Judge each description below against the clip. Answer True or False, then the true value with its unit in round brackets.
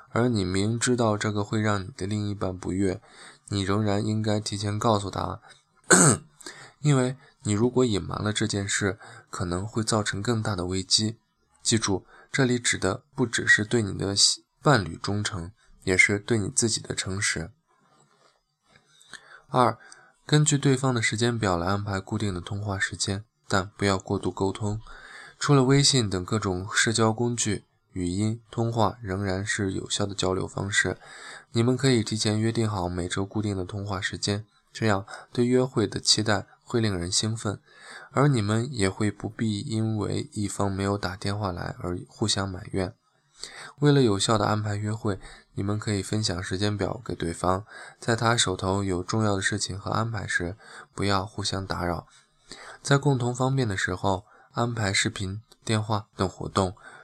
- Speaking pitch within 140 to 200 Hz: False (105 Hz)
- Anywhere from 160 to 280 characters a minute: True (245 characters per minute)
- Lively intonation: False (3.0 semitones)